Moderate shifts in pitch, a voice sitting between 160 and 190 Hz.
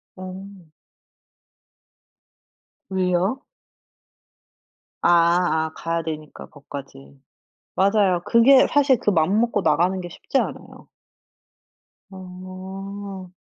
Yes: average, 3.0 semitones; medium, 185 Hz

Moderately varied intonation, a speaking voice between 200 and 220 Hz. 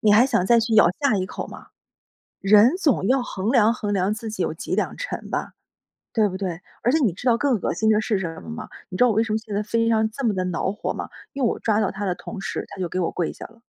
Yes: average, 3.5 semitones; high, 215 Hz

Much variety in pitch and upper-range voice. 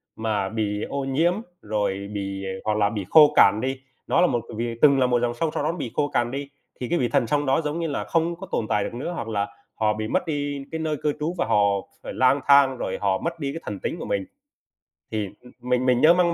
No: wide, 5.7 semitones; low, 125 Hz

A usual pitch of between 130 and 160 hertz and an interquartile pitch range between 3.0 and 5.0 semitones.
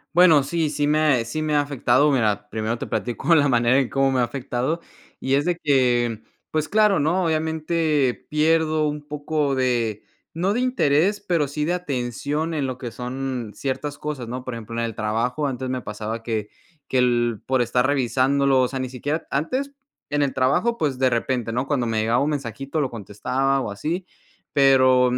Yes: low, 135 Hz; average, 3.8 semitones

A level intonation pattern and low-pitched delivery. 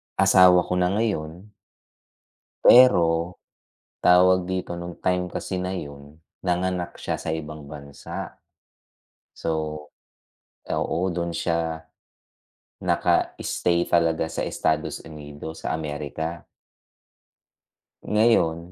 Yes: narrow, 2.3 semitones; very low, 85 Hz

